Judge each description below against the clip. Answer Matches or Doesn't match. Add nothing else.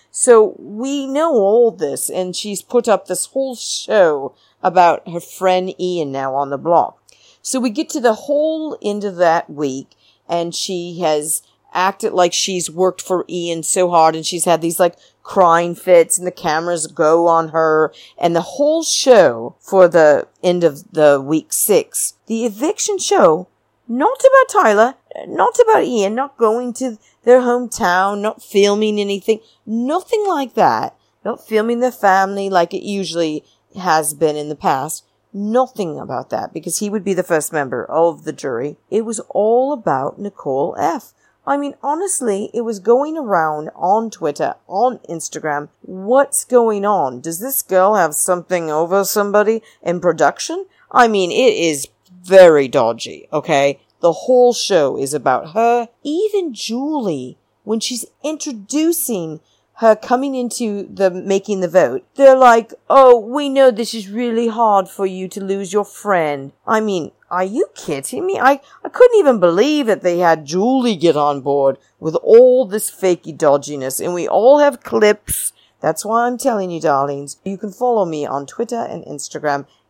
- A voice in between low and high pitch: Doesn't match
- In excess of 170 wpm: Doesn't match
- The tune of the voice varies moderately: Doesn't match